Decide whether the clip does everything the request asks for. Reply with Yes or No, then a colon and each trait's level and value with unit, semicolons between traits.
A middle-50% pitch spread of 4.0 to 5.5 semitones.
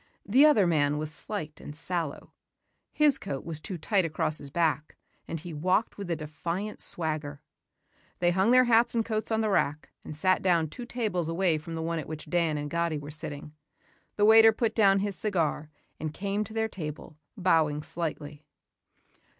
Yes: average, 5.1 semitones